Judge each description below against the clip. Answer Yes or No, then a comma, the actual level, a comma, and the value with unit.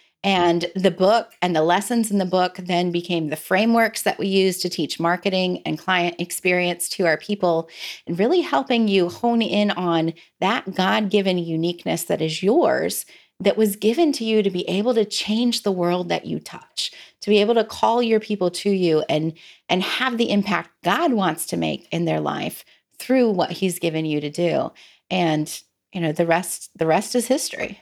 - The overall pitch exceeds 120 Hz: Yes, medium, 185 Hz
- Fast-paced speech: No, average, 195 wpm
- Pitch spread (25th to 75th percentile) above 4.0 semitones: No, average, 3.4 semitones